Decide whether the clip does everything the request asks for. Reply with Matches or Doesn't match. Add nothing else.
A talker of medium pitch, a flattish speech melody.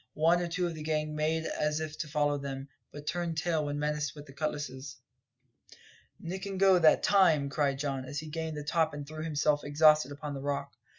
Matches